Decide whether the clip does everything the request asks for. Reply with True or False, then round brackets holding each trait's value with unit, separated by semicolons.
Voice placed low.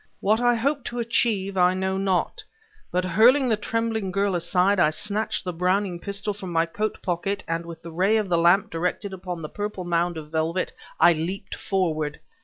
False (190 Hz)